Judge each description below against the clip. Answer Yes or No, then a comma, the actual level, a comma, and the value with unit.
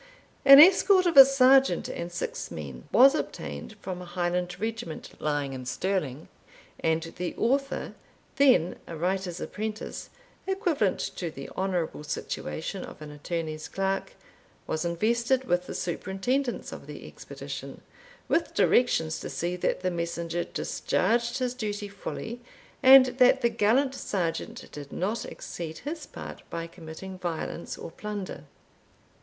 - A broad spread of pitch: Yes, wide, 6.6 semitones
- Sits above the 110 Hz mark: Yes, high, 190 Hz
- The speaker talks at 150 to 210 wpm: No, average, 140 wpm